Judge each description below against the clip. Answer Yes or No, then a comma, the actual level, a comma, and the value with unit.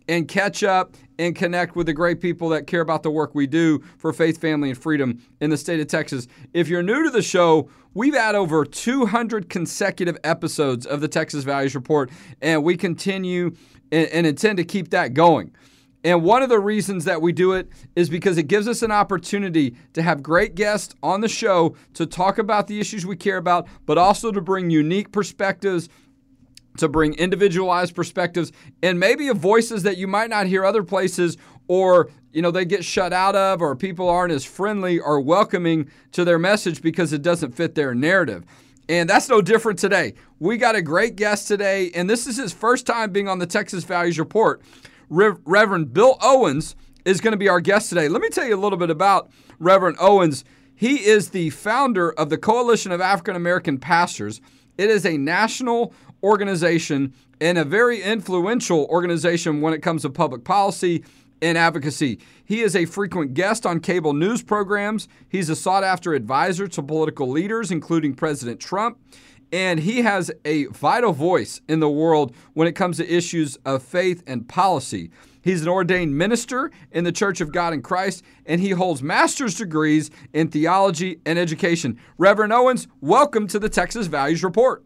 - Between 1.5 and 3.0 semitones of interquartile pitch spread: No, average, 4.2 semitones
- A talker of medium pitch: Yes, medium, 175 Hz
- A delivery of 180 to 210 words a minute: Yes, average, 190 wpm